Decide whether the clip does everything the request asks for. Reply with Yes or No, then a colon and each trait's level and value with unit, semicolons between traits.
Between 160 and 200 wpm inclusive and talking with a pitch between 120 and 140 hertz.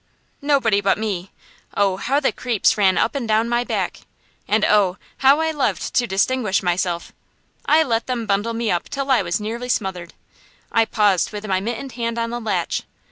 No: average, 190 wpm; high, 225 Hz